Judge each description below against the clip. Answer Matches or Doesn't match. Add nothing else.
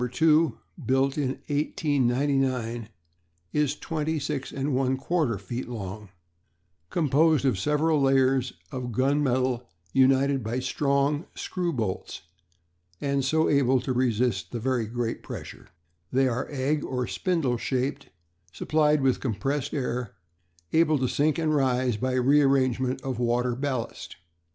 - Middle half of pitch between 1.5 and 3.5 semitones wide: Matches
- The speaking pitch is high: Doesn't match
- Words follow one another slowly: Matches